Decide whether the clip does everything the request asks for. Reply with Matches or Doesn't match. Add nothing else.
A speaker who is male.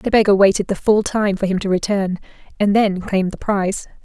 Doesn't match